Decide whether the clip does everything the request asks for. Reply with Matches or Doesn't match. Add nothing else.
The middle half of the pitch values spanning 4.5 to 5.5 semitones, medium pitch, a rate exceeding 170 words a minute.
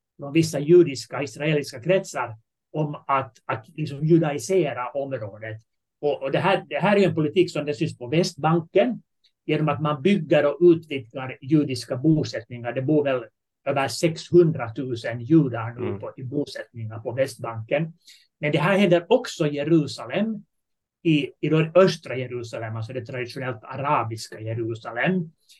Doesn't match